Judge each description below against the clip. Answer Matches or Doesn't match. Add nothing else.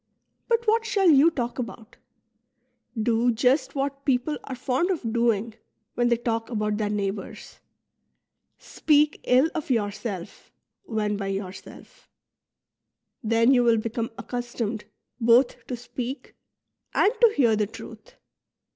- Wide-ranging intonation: Doesn't match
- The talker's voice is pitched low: Doesn't match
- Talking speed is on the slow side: Matches